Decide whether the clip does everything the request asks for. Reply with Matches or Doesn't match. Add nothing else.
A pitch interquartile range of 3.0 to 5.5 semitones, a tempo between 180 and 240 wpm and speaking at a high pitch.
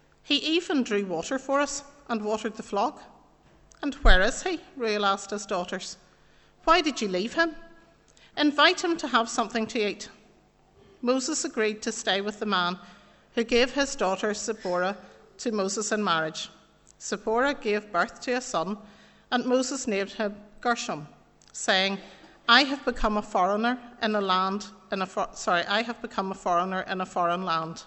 Doesn't match